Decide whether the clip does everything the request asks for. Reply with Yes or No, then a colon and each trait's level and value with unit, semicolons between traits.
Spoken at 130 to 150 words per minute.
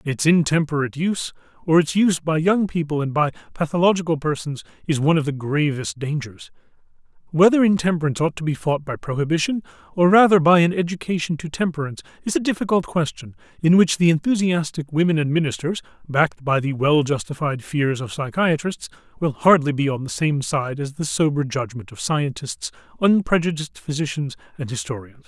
No: average, 165 wpm